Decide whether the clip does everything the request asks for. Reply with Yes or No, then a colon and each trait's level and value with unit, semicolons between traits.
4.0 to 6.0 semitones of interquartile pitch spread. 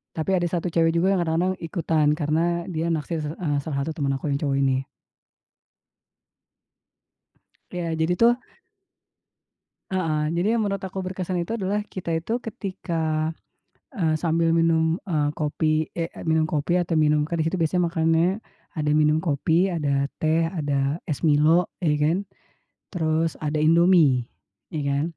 No: narrow, 2.5 semitones